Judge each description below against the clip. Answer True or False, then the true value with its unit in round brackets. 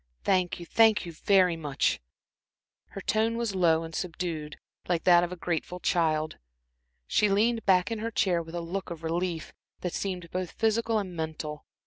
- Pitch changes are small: False (3.2 semitones)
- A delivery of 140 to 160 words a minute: False (175 wpm)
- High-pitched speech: False (180 Hz)